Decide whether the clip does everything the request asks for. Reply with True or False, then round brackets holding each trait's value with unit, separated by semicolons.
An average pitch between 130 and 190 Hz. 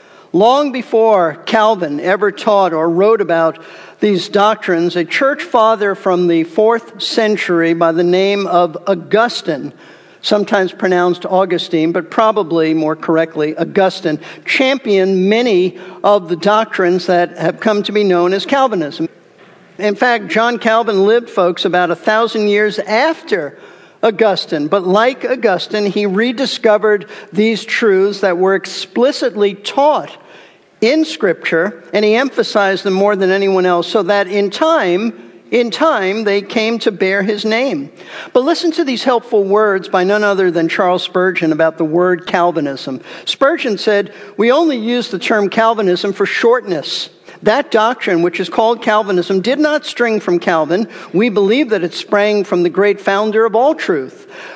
False (205 Hz)